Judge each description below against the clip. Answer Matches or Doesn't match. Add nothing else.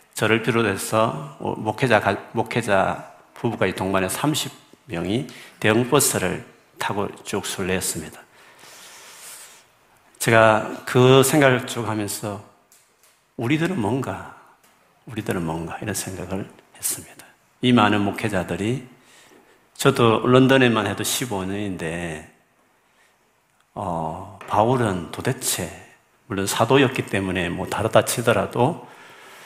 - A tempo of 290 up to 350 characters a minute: Doesn't match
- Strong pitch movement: Doesn't match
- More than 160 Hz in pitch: Doesn't match